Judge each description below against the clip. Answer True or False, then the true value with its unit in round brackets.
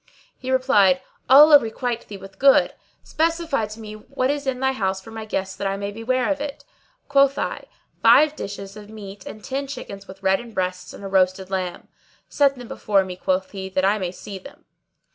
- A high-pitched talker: True (215 Hz)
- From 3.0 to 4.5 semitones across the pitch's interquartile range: False (5.5 semitones)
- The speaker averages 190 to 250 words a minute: True (205 wpm)